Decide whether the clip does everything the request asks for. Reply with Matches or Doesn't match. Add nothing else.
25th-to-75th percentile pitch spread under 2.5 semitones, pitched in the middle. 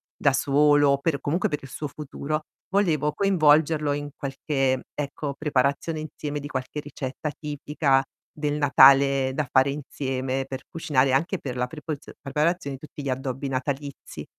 Matches